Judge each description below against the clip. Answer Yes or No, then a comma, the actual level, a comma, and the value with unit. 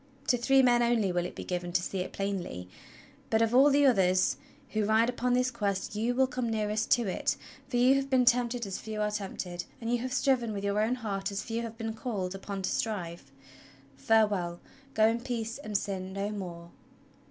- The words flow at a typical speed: No, fast, 210 wpm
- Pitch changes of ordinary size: Yes, average, 3.8 semitones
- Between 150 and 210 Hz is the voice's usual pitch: No, high, 220 Hz